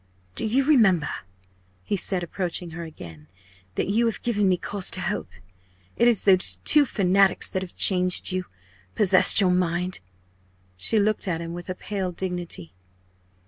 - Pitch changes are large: No, average, 2.8 semitones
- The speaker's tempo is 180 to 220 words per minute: No, average, 160 wpm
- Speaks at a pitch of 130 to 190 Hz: Yes, medium, 185 Hz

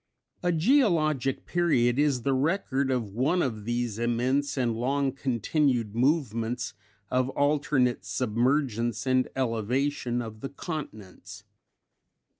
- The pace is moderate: No, slow, 115 wpm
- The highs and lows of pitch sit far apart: No, average, 3.4 semitones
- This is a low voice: Yes, low, 130 Hz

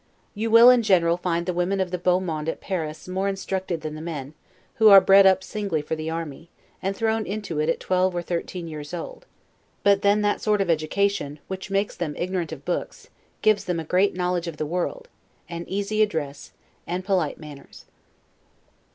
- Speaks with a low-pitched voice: No, medium, 180 Hz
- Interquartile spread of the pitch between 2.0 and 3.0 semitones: No, average, 3.4 semitones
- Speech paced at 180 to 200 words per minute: Yes, average, 195 wpm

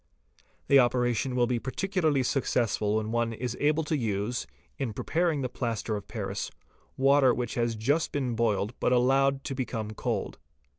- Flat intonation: No, average, 3.1 semitones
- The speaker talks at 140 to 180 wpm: Yes, average, 160 wpm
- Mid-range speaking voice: No, low, 125 Hz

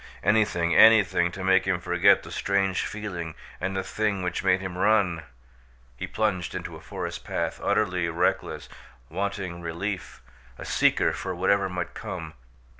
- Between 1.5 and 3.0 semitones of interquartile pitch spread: Yes, narrow, 2.4 semitones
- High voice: No, very low, 95 Hz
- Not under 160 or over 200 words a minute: No, average, 150 wpm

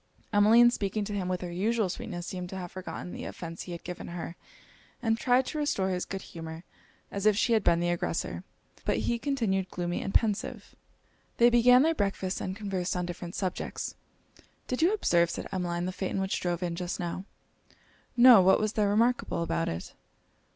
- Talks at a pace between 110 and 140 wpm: No, average, 195 wpm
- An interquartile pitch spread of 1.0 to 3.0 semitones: No, average, 4.1 semitones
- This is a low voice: No, high, 190 Hz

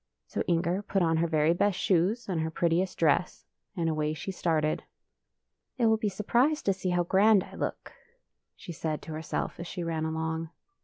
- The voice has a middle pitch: Yes, medium, 170 Hz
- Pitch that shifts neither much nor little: Yes, average, 3.2 semitones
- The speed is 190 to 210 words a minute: Yes, average, 195 wpm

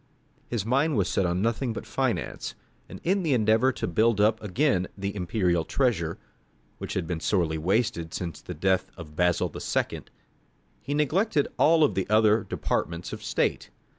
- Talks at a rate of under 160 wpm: No, average, 165 wpm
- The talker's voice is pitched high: No, low, 105 Hz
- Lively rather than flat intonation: Yes, wide, 6.1 semitones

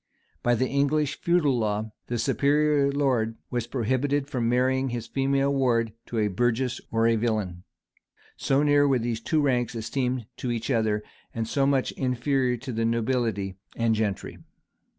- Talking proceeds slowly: No, average, 165 wpm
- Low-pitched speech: Yes, low, 125 Hz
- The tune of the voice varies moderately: Yes, average, 3.3 semitones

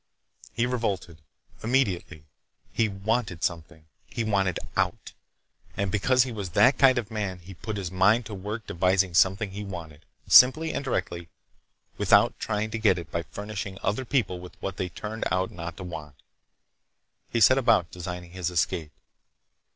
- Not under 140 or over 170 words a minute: Yes, average, 160 wpm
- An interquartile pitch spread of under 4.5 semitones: Yes, average, 4.1 semitones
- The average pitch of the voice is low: Yes, very low, 95 Hz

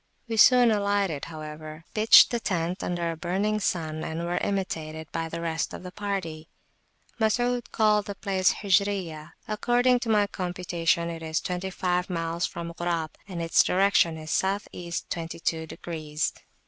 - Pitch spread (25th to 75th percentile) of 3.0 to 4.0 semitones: Yes, average, 3.6 semitones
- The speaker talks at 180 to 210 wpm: No, average, 160 wpm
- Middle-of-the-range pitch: Yes, medium, 175 Hz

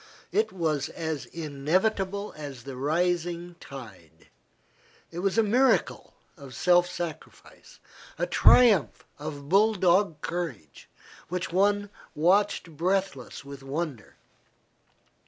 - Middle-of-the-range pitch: Yes, medium, 170 Hz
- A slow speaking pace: Yes, slow, 105 wpm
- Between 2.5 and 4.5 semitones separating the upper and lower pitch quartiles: No, average, 5.3 semitones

